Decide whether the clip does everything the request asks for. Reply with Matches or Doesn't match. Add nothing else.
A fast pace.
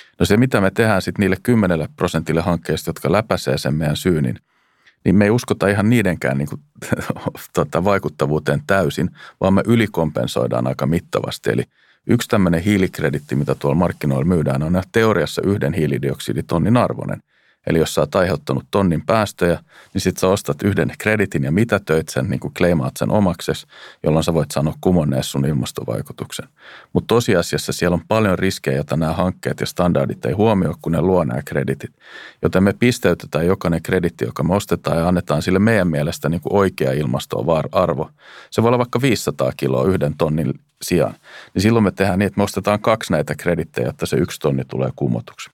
Matches